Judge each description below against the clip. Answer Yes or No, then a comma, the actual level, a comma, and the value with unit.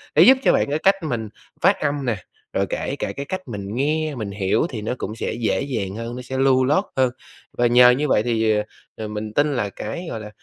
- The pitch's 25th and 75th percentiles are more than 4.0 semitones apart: Yes, average, 4.6 semitones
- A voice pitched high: No, low, 125 Hz